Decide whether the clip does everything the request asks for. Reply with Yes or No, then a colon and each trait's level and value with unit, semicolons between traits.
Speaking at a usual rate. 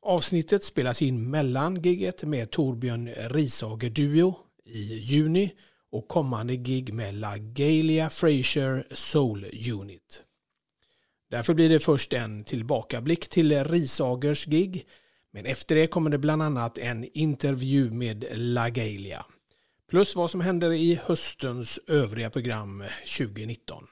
No: slow, 120 wpm